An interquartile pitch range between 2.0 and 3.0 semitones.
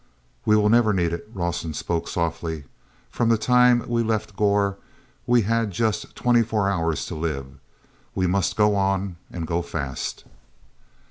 No: average, 4.6 semitones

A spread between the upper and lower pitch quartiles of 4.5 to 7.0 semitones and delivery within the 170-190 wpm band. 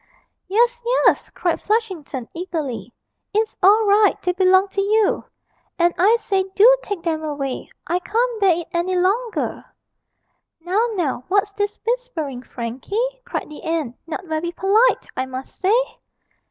No: average, 5.1 semitones; average, 145 wpm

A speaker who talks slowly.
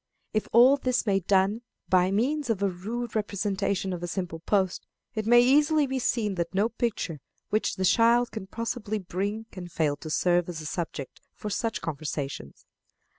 No: average, 175 wpm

